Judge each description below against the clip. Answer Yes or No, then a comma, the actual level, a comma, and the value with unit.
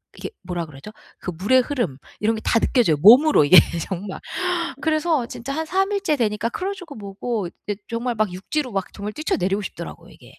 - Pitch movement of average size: No, wide, 7.0 semitones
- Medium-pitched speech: No, high, 225 Hz